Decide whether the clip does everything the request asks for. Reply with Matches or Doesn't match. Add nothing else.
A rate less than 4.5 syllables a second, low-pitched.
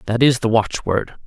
Doesn't match